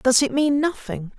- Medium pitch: No, very high, 260 Hz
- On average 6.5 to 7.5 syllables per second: No, 4.5 syllables/s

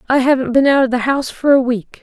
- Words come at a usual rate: No, fast, 295 wpm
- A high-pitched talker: Yes, very high, 260 Hz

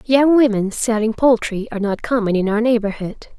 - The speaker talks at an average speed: Yes, average, 175 wpm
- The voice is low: No, high, 225 Hz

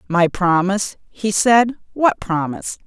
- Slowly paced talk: Yes, slow, 125 wpm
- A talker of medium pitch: No, high, 195 Hz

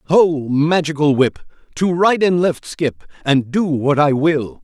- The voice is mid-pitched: Yes, medium, 155 Hz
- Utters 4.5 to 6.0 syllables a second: No, 3.8 syllables/s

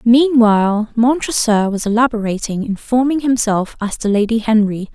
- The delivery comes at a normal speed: No, slow, 120 wpm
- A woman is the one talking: Yes, female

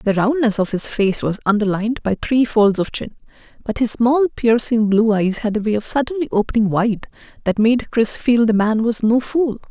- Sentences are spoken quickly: Yes, fast, 210 wpm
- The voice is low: No, high, 225 Hz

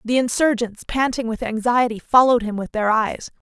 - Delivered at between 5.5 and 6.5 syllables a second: No, 5.3 syllables/s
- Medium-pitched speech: No, high, 235 Hz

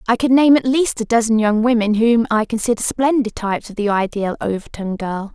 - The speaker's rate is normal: No, fast, 215 wpm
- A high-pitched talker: Yes, high, 225 Hz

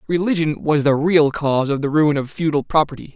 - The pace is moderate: No, fast, 210 wpm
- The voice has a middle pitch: Yes, medium, 150 Hz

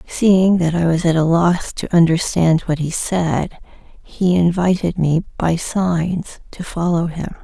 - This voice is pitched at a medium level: Yes, medium, 170 Hz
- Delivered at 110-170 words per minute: Yes, average, 160 wpm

